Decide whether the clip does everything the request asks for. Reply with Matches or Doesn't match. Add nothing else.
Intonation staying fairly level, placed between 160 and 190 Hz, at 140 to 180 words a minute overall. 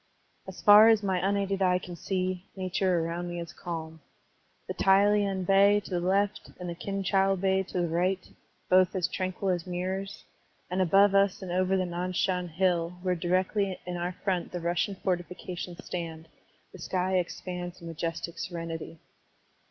Matches